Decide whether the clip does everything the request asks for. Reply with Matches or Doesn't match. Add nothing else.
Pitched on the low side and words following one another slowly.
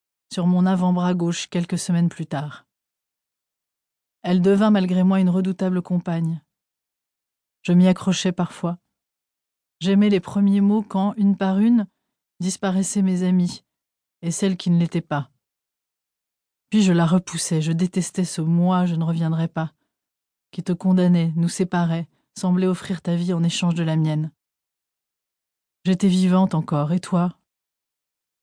Doesn't match